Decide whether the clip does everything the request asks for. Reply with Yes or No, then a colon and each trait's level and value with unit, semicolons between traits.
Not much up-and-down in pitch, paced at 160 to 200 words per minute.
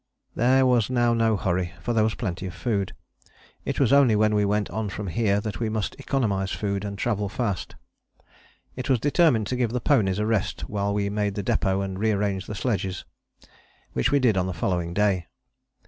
No: average, 3.2 semitones; average, 195 wpm